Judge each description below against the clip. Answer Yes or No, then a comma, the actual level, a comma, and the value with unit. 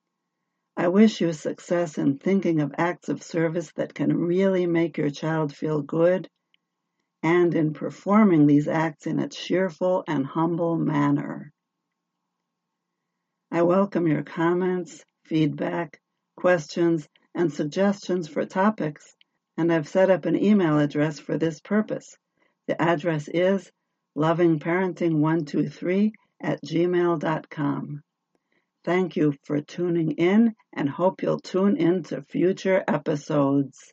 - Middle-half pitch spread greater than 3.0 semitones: No, average, 2.7 semitones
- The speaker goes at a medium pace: No, slow, 120 wpm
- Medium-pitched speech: Yes, medium, 170 Hz